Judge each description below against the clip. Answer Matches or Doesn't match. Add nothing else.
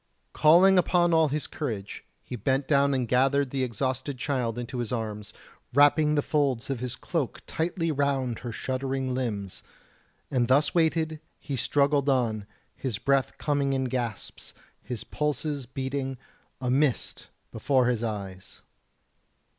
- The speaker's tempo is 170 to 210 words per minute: Doesn't match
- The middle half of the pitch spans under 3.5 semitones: Matches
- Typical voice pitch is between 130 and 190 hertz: Matches